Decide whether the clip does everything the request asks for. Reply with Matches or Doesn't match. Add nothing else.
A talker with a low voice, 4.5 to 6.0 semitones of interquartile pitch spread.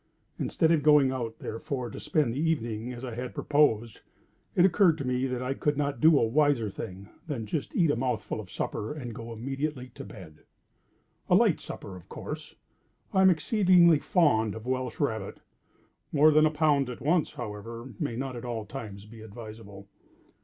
Matches